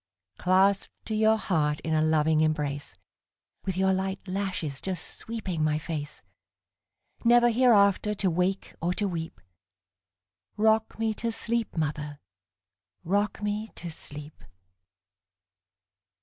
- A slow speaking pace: Yes, slow, 105 wpm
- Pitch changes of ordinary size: No, wide, 5.7 semitones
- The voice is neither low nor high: Yes, medium, 175 Hz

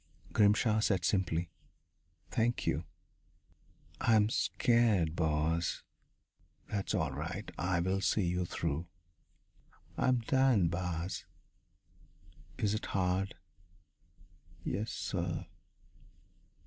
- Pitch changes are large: No, average, 4.1 semitones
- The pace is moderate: No, slow, 80 wpm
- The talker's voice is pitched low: Yes, very low, 95 Hz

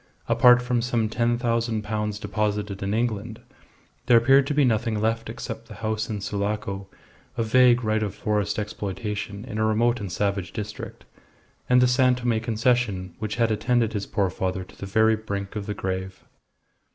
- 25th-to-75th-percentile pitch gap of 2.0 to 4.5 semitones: Yes, narrow, 2.5 semitones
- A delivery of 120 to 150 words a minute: No, average, 175 wpm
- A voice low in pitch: Yes, low, 110 Hz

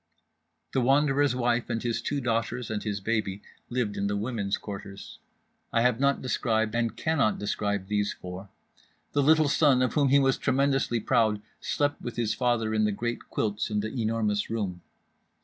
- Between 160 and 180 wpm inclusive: Yes, average, 175 wpm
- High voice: No, low, 115 Hz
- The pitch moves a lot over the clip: No, average, 3.7 semitones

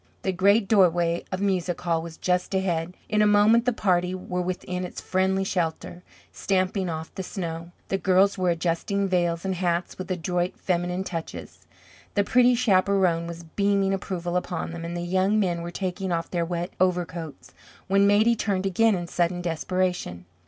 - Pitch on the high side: No, medium, 180 Hz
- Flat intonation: Yes, narrow, 2.1 semitones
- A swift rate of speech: No, average, 175 wpm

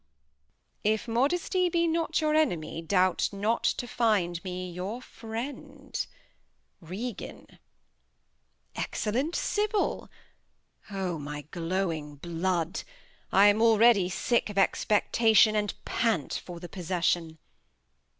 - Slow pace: Yes, slow, 105 wpm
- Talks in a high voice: Yes, high, 205 Hz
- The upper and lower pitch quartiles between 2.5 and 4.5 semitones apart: No, average, 5.3 semitones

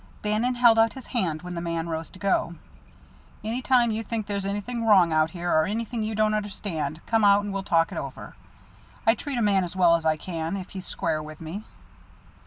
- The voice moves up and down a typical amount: Yes, average, 4.7 semitones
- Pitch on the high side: Yes, high, 200 Hz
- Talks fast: Yes, fast, 220 wpm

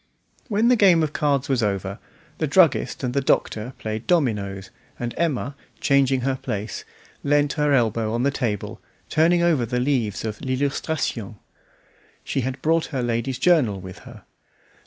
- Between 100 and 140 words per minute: No, average, 155 wpm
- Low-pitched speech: Yes, low, 130 Hz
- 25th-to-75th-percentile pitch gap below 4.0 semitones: No, average, 4.8 semitones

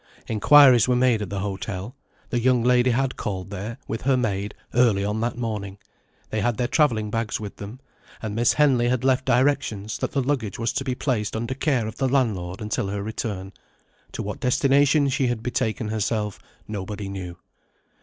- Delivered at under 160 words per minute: No, average, 185 wpm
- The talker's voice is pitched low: Yes, low, 115 Hz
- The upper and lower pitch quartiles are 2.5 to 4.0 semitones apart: Yes, average, 3.6 semitones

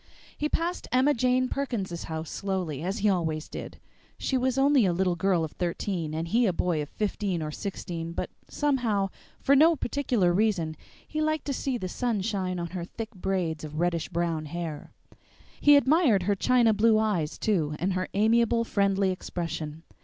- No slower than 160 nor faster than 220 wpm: Yes, average, 180 wpm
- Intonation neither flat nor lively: No, wide, 5.8 semitones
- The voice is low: No, high, 195 Hz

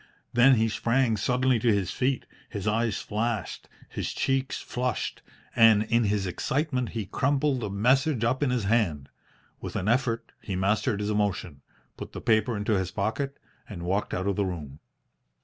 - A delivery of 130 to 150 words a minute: No, average, 170 wpm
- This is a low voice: Yes, low, 110 Hz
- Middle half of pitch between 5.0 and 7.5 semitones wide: No, average, 3.9 semitones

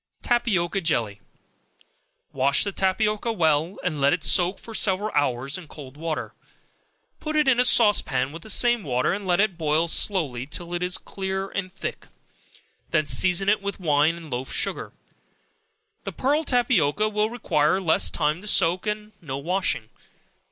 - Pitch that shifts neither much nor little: No, wide, 5.7 semitones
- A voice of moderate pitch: Yes, medium, 180 Hz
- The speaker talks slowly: No, average, 165 wpm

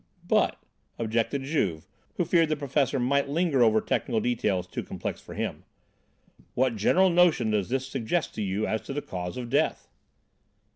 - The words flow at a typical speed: Yes, average, 165 wpm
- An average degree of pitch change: Yes, average, 4.8 semitones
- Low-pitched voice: Yes, low, 125 Hz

